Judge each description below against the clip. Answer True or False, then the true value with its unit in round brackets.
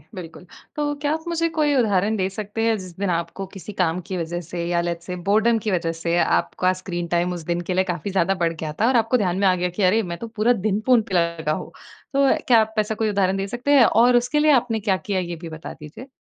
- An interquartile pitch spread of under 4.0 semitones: False (4.7 semitones)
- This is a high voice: True (195 Hz)